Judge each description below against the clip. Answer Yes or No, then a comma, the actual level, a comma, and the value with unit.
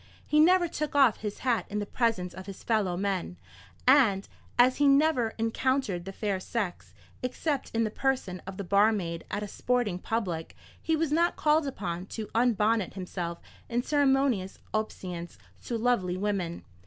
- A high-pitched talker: Yes, high, 220 Hz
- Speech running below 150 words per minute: No, average, 165 wpm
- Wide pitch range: Yes, wide, 5.7 semitones